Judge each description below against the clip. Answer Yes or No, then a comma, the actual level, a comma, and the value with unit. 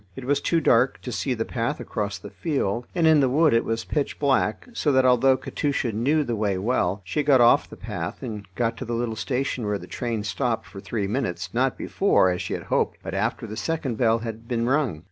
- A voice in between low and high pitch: No, low, 120 Hz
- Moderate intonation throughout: Yes, average, 4.0 semitones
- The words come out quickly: Yes, fast, 235 wpm